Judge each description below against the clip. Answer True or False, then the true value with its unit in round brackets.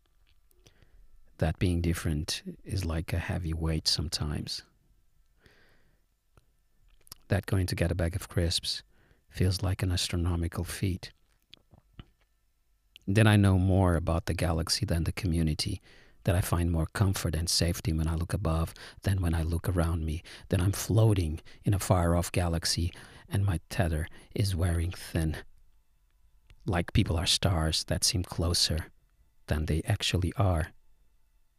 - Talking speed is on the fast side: False (140 wpm)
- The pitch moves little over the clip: False (3.1 semitones)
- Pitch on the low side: True (90 Hz)